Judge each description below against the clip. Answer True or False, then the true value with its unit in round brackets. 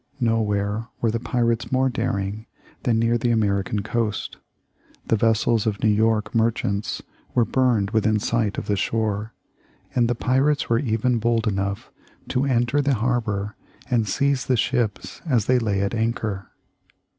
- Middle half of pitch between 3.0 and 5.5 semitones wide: False (2.5 semitones)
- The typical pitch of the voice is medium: False (115 Hz)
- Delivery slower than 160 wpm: True (150 wpm)